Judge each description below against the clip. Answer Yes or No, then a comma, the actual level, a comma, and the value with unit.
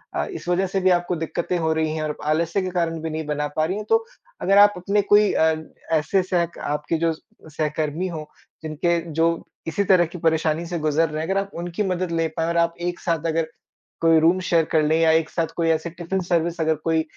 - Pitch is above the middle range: No, medium, 165 Hz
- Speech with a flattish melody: Yes, narrow, 2.0 semitones